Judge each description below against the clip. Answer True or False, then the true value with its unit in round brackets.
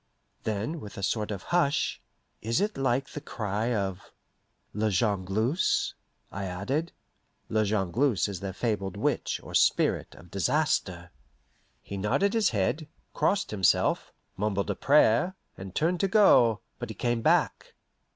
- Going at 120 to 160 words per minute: True (135 wpm)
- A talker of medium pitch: False (110 Hz)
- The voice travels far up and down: True (6.6 semitones)